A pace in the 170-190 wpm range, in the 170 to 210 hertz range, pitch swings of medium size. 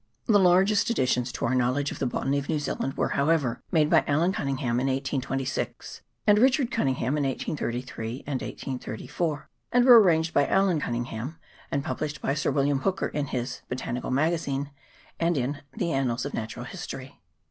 No: average, 180 wpm; medium, 140 Hz; average, 4.1 semitones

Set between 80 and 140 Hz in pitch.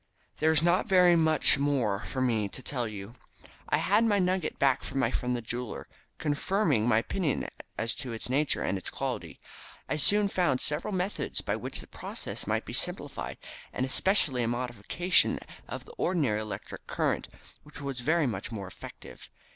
Yes: low, 135 Hz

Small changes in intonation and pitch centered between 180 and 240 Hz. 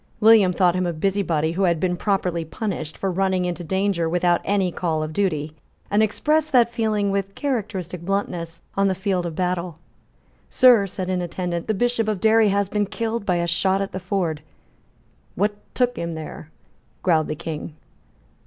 No: average, 3.1 semitones; medium, 185 Hz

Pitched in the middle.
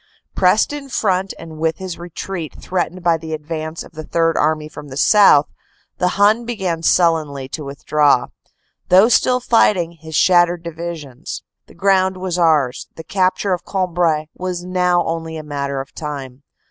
Yes: medium, 170 Hz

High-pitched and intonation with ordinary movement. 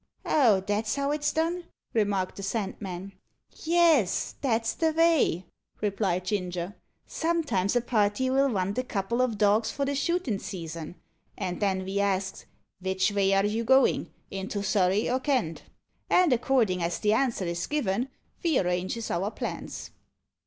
No: high, 210 Hz; wide, 5.8 semitones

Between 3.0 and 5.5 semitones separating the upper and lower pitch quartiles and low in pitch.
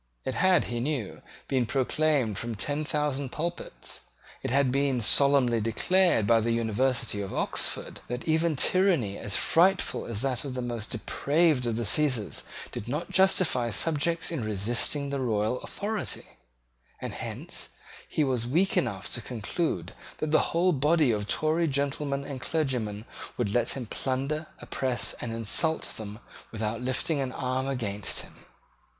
Yes: average, 5.0 semitones; low, 130 Hz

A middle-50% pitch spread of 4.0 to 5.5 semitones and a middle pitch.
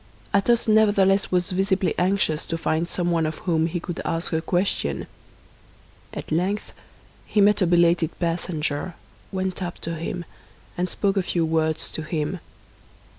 No: average, 2.8 semitones; medium, 175 Hz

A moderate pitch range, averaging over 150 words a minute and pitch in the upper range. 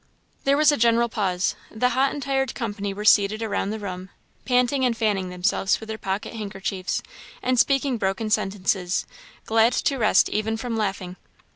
Yes: average, 4.2 semitones; average, 170 wpm; high, 220 Hz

